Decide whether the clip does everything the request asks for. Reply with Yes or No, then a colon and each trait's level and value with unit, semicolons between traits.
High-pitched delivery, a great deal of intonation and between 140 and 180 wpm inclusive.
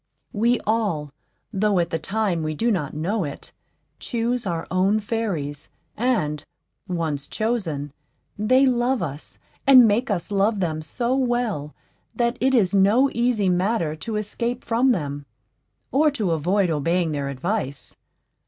Yes: high, 200 Hz; wide, 6.7 semitones; average, 145 wpm